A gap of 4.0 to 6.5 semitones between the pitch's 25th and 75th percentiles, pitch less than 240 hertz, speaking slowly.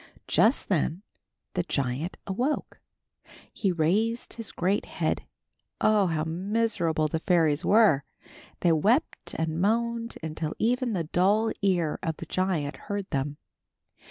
Yes: average, 5.3 semitones; medium, 185 Hz; slow, 130 wpm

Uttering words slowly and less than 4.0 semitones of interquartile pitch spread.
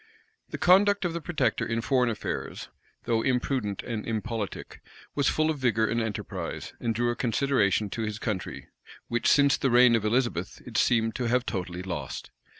No: average, 175 wpm; average, 3.4 semitones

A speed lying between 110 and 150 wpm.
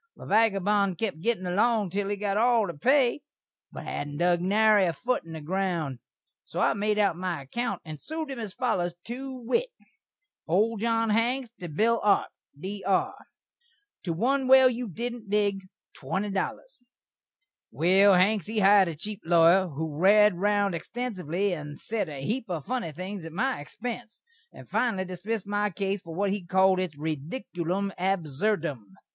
No: average, 165 wpm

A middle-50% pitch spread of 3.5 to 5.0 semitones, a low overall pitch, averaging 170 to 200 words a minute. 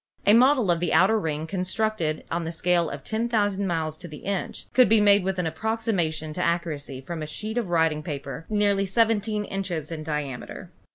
No: average, 4.7 semitones; medium, 180 Hz; average, 190 wpm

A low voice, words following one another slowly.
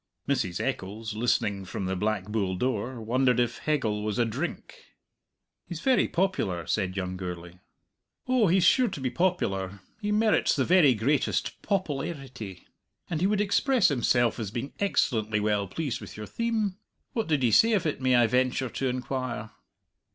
No: low, 125 Hz; average, 170 wpm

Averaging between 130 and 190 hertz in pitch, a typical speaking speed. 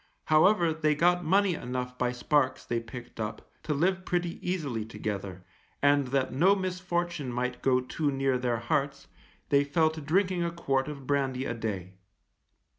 Yes: medium, 140 Hz; average, 165 wpm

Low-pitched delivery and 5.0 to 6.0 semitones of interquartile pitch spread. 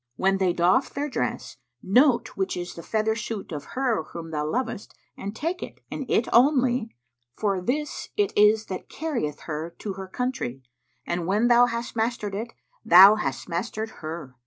No: high, 215 Hz; wide, 5.6 semitones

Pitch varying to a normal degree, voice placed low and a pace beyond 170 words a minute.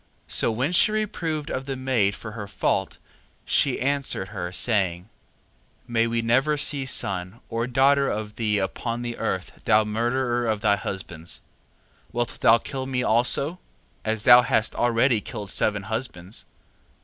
No: average, 3.9 semitones; low, 115 Hz; average, 155 wpm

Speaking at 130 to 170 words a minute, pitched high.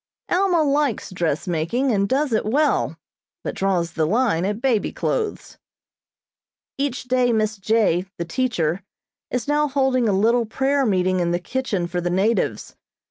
Yes: average, 150 wpm; high, 220 Hz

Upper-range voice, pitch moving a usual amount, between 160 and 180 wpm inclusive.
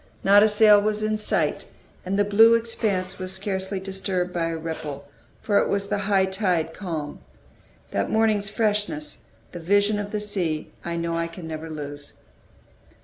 Yes: high, 195 Hz; average, 3.8 semitones; average, 170 wpm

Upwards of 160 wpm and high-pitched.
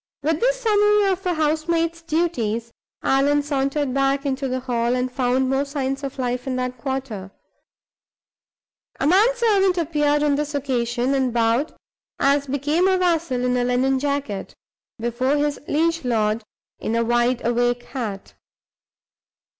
No: average, 145 wpm; very high, 275 Hz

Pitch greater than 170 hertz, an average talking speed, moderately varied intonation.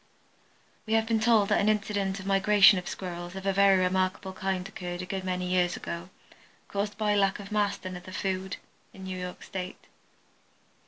No: high, 190 Hz; average, 190 wpm; narrow, 1.6 semitones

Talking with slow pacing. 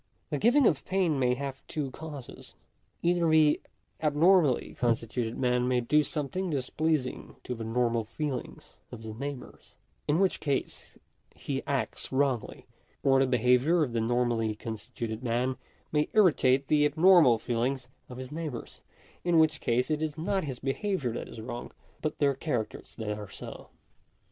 No: average, 160 wpm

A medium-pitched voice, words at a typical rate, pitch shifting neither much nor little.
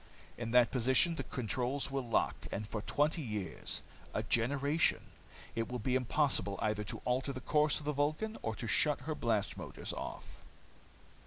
No: low, 130 Hz; average, 170 wpm; average, 4.3 semitones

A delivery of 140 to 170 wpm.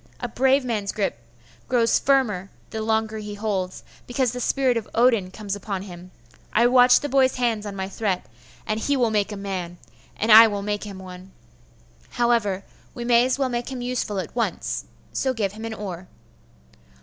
No: average, 190 wpm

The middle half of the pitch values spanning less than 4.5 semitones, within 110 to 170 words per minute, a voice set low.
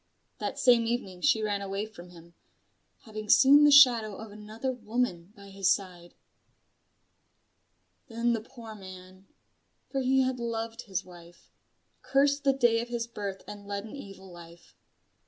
No: average, 4.0 semitones; average, 155 wpm; high, 215 Hz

